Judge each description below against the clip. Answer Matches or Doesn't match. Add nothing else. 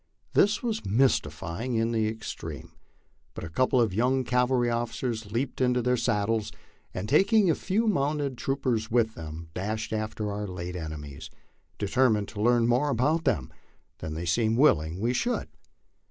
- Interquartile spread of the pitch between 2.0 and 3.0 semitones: Doesn't match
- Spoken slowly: Doesn't match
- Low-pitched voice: Matches